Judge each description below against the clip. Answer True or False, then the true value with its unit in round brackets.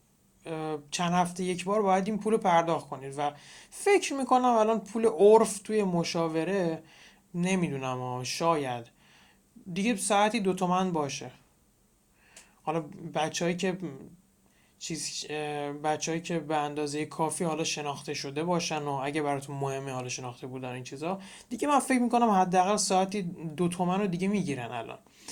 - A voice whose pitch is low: False (165 Hz)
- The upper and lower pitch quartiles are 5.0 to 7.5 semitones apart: False (4.6 semitones)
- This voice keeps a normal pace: True (140 wpm)